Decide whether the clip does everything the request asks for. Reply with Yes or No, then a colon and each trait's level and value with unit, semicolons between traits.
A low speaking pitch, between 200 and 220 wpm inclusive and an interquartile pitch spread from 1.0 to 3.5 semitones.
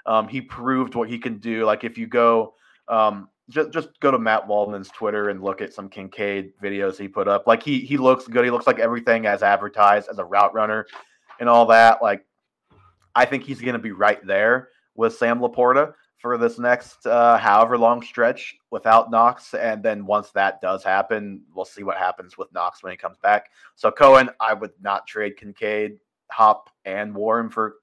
Yes: low, 115 Hz; fast, 205 wpm; average, 2.9 semitones